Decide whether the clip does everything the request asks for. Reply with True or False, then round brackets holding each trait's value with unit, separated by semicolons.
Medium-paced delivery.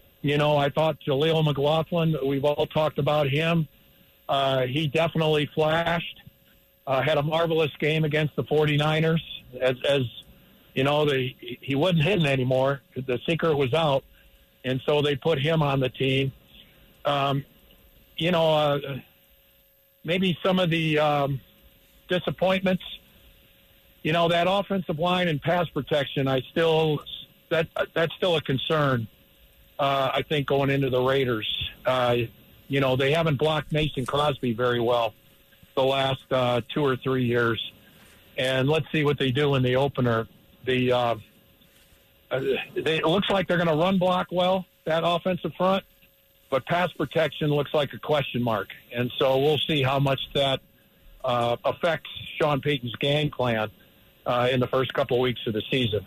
True (160 wpm)